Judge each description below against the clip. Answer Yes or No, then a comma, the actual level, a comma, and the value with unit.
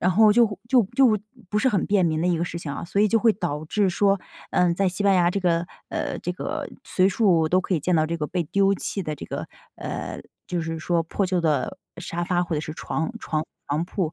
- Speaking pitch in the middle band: Yes, medium, 180 Hz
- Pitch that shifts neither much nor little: Yes, average, 3.3 semitones